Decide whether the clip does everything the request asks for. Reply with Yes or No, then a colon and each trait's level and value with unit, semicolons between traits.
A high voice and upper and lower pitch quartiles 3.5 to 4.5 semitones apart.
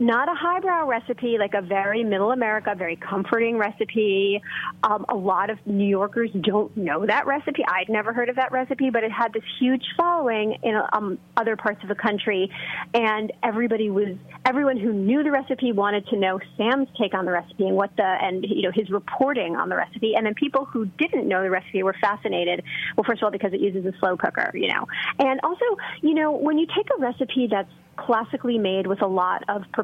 Yes: high, 220 Hz; average, 4.0 semitones